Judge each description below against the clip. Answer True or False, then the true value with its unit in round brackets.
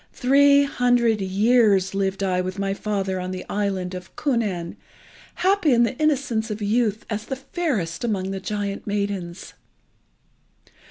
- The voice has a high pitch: True (205 Hz)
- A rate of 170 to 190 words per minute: False (145 wpm)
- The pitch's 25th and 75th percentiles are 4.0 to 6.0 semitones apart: True (4.3 semitones)